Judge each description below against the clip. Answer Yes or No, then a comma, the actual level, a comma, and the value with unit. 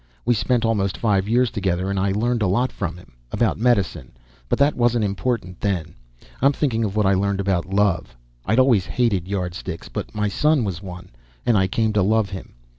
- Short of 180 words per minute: No, average, 200 wpm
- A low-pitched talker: Yes, low, 100 Hz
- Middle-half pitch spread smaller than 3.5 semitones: No, average, 3.8 semitones